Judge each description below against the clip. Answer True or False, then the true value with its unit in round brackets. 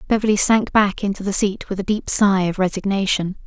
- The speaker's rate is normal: False (210 wpm)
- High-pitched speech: True (200 Hz)